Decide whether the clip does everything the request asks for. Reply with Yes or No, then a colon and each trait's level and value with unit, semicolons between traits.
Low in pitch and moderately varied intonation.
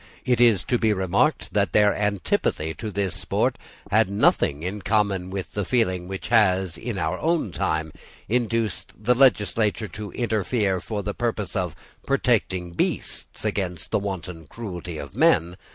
Yes: low, 100 Hz; average, 3.6 semitones